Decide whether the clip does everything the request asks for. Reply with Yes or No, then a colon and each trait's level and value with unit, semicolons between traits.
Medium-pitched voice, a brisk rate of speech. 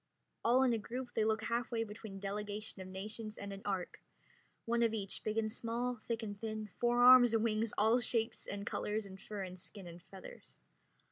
No: high, 215 Hz; fast, 210 wpm